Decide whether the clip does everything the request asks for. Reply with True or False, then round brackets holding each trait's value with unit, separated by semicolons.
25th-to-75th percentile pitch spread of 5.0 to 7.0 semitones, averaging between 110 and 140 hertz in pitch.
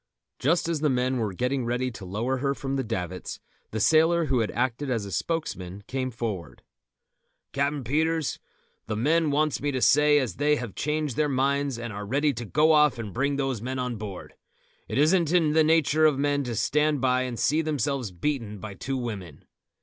False (4.4 semitones; 135 Hz)